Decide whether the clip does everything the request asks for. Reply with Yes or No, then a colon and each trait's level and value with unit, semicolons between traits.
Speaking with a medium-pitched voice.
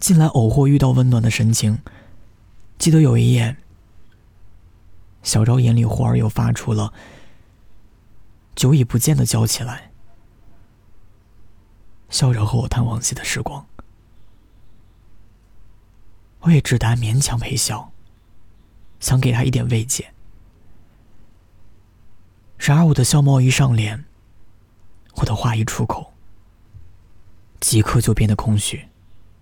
No: low, 110 Hz